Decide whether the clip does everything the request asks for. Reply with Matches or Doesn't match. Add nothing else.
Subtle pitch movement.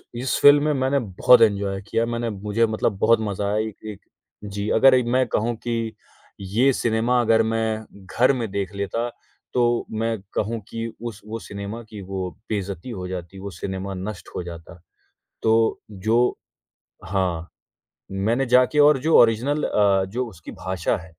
Doesn't match